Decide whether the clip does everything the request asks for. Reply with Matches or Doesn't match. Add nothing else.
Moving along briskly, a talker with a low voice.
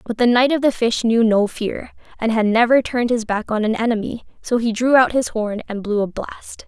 Doesn't match